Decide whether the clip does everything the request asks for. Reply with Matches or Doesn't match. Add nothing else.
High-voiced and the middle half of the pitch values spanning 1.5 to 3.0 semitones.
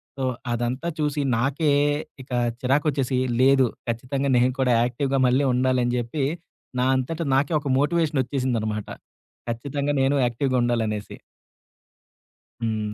Doesn't match